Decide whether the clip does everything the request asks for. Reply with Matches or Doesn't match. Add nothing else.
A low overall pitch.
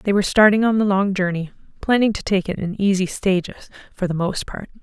Doesn't match